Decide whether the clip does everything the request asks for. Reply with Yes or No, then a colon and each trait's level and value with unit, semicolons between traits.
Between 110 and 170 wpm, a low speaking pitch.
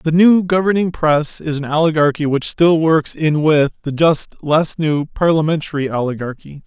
No: average, 160 wpm; medium, 155 Hz